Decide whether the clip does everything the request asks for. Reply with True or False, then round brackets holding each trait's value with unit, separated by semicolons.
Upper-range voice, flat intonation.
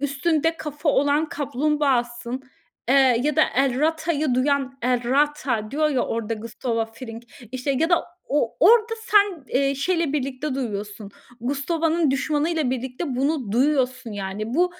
False (275 Hz; 3.7 semitones)